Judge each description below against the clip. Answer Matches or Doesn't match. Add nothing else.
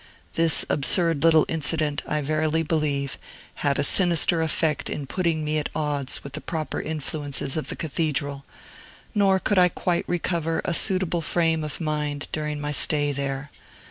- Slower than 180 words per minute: Matches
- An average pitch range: Doesn't match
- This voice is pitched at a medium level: Matches